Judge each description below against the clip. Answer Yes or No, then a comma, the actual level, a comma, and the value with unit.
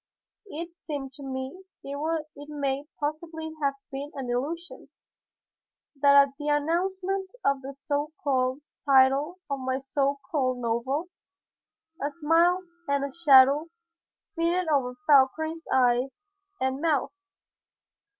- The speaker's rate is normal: No, slow, 120 wpm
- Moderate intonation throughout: Yes, average, 3.2 semitones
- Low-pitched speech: No, very high, 285 Hz